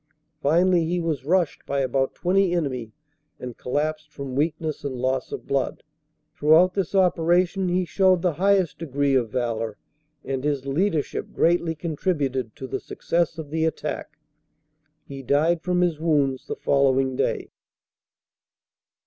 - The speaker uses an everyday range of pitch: Yes, average, 4.3 semitones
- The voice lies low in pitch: No, medium, 155 Hz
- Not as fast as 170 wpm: Yes, average, 140 wpm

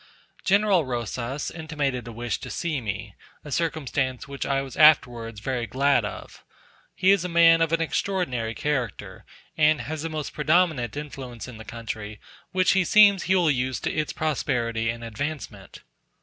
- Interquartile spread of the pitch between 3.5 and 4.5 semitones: No, wide, 5.4 semitones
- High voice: No, medium, 140 Hz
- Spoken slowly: No, average, 165 wpm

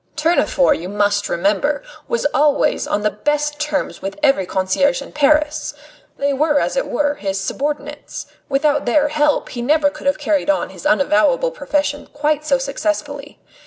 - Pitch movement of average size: No, narrow, 2.1 semitones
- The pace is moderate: Yes, average, 160 wpm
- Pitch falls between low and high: No, very high, 290 Hz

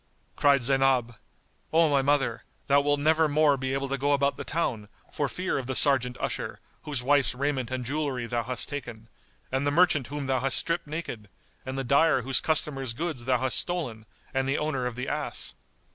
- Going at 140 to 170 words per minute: No, average, 200 wpm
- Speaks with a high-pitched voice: No, low, 135 Hz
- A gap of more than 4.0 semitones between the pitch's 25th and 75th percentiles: No, narrow, 2.5 semitones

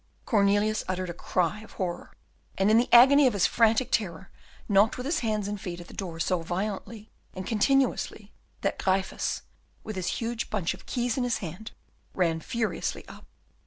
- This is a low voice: No, high, 205 Hz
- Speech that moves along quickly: No, average, 180 wpm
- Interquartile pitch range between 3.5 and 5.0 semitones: Yes, average, 3.8 semitones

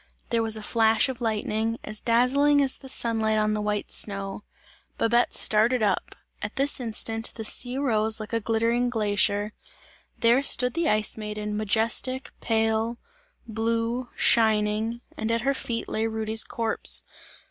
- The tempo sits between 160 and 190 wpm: No, average, 150 wpm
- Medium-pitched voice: No, high, 225 Hz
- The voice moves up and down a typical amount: No, narrow, 1.8 semitones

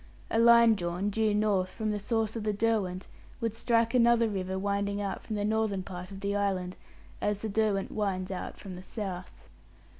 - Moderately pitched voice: No, high, 205 Hz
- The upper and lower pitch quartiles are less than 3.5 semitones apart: Yes, narrow, 2.6 semitones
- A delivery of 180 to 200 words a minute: Yes, average, 190 wpm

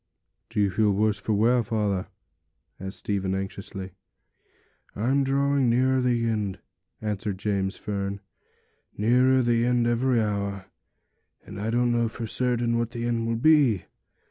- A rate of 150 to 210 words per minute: No, slow, 135 wpm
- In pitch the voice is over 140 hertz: No, low, 115 Hz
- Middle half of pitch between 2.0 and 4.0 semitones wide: Yes, average, 3.2 semitones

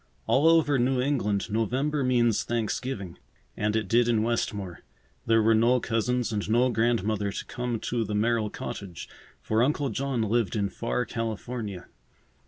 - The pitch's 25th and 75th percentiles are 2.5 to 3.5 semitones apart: Yes, average, 2.8 semitones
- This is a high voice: No, low, 115 Hz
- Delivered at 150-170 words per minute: Yes, average, 155 wpm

